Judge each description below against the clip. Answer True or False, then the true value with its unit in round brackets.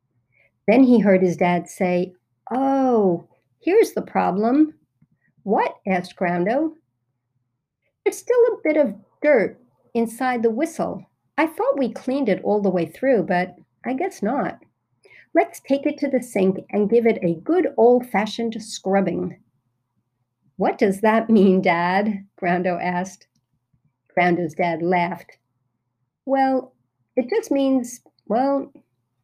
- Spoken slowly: True (130 wpm)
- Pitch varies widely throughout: True (7.3 semitones)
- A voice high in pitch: True (195 Hz)